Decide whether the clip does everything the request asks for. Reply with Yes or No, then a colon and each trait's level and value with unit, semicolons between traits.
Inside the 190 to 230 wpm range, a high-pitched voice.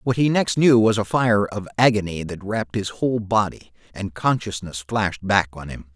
No: average, 200 wpm; low, 105 Hz